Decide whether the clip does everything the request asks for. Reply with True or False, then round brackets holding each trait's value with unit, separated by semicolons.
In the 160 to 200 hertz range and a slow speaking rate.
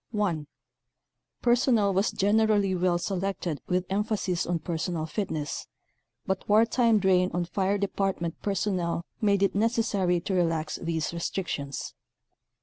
True (190 Hz; 125 wpm)